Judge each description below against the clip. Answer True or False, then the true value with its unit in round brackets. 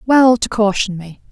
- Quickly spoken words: False (185 wpm)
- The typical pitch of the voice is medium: False (215 Hz)